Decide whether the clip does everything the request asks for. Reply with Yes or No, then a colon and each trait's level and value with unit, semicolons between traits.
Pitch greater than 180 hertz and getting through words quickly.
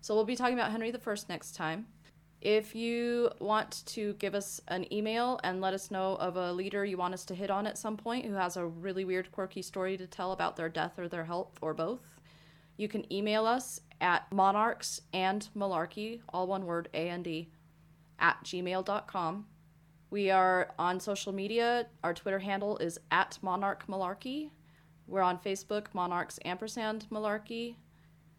No: high, 190 Hz; average, 165 wpm